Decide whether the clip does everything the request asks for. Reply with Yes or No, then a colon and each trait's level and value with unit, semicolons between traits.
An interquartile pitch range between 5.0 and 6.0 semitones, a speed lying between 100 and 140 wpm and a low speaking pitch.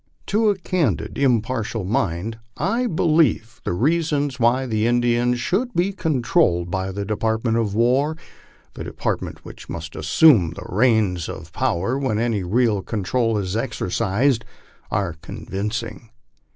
Yes: wide, 5.5 semitones; slow, 135 wpm; low, 115 Hz